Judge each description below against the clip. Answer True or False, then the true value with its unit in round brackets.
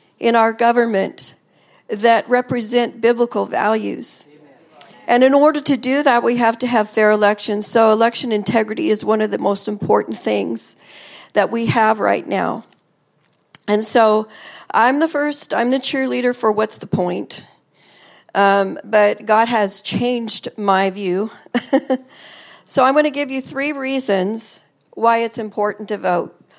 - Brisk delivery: False (150 wpm)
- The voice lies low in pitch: False (225 Hz)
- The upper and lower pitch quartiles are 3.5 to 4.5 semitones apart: False (2.9 semitones)